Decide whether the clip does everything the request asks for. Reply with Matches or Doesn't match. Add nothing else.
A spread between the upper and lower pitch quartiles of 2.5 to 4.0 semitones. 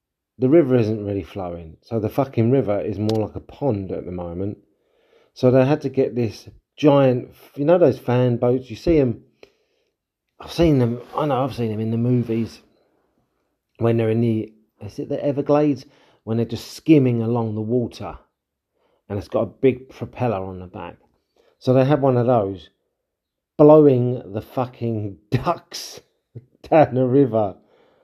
Doesn't match